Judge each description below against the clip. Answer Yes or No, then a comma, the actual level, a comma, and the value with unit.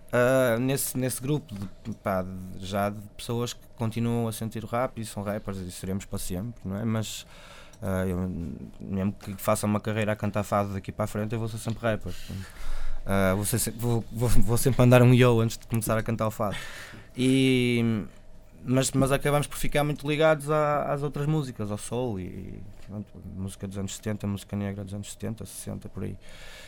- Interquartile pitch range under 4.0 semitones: Yes, average, 3.3 semitones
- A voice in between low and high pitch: No, low, 105 Hz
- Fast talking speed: Yes, fast, 200 wpm